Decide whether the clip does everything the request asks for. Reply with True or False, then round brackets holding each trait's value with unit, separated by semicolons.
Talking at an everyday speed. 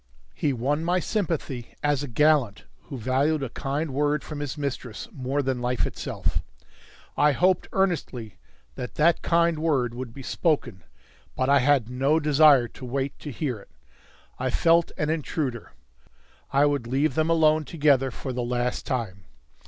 True (160 wpm)